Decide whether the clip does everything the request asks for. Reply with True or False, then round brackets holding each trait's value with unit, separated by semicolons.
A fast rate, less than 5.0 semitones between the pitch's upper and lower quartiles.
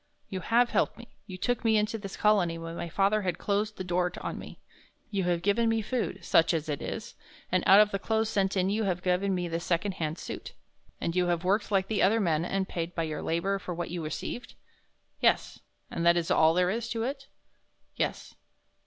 True (225 wpm; 3.6 semitones)